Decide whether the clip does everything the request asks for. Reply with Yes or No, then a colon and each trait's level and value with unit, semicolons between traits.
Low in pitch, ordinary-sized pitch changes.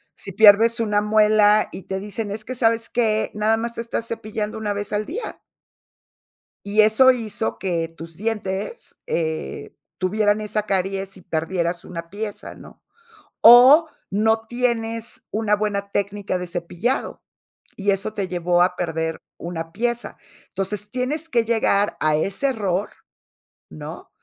No: high, 210 Hz; average, 3.1 semitones